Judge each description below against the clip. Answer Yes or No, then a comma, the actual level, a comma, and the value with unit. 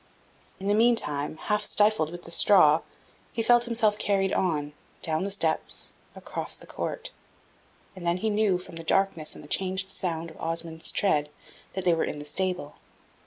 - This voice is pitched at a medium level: Yes, medium, 180 Hz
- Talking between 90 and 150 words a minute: No, average, 175 wpm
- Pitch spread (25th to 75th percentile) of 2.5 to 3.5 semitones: No, average, 4.0 semitones